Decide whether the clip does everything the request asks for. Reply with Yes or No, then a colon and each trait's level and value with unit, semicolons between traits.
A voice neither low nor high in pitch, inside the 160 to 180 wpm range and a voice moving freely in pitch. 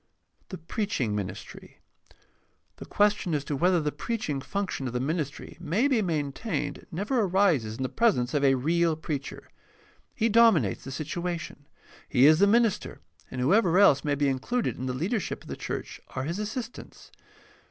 Yes: medium, 165 Hz; average, 175 wpm; wide, 7.0 semitones